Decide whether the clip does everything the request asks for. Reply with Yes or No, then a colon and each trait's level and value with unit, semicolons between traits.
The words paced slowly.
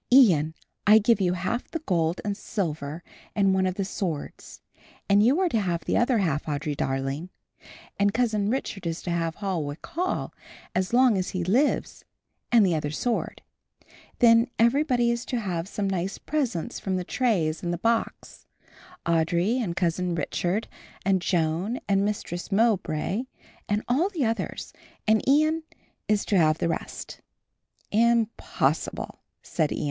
No: average, 155 wpm